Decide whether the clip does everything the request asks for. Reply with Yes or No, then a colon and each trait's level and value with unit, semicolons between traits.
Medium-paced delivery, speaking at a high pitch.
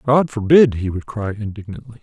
No: average, 180 wpm; low, 115 Hz